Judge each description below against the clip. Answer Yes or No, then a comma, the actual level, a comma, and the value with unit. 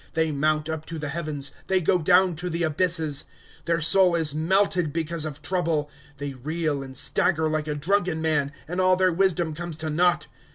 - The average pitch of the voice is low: No, medium, 160 Hz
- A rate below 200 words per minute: No, fast, 205 wpm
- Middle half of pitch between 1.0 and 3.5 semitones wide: Yes, average, 2.7 semitones